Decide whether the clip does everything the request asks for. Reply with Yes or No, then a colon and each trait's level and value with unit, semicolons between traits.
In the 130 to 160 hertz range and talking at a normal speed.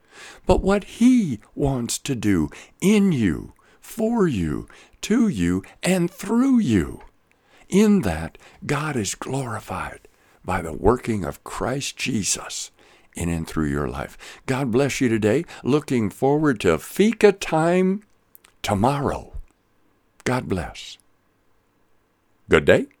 No: low, 135 Hz; slow, 115 wpm